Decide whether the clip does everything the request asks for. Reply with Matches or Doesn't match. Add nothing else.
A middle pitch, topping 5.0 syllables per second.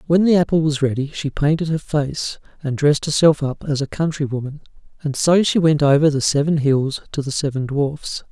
Matches